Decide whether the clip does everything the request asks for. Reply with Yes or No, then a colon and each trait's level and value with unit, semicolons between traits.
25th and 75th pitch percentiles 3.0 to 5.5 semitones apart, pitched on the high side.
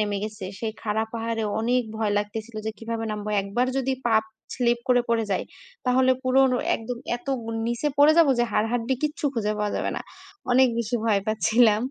No: narrow, 2.4 semitones; high, 230 Hz